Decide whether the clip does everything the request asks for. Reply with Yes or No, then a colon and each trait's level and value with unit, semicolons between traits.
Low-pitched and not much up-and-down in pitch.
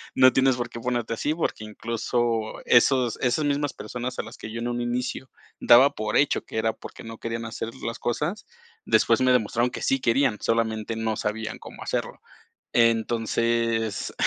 Yes: low, 115 Hz; narrow, 2.0 semitones